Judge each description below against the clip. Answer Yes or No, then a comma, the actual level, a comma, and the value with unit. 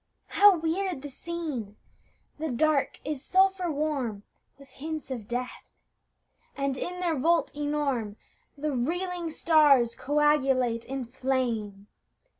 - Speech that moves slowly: Yes, slow, 115 wpm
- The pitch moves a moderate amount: Yes, average, 4.2 semitones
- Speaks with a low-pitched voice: No, very high, 290 Hz